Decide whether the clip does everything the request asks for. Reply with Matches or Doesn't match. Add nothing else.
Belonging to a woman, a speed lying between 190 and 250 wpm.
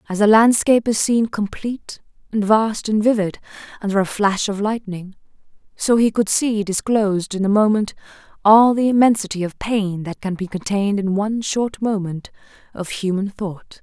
Doesn't match